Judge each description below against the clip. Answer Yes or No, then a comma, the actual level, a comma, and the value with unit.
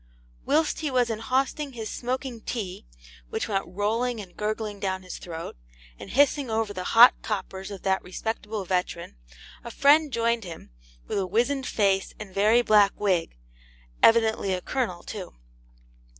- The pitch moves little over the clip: No, average, 4.1 semitones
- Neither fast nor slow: Yes, average, 150 wpm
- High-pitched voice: Yes, high, 215 Hz